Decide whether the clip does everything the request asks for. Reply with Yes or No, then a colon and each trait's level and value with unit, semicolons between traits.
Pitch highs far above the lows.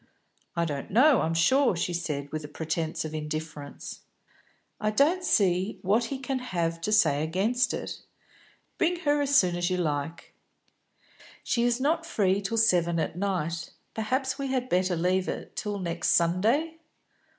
Yes: wide, 7.0 semitones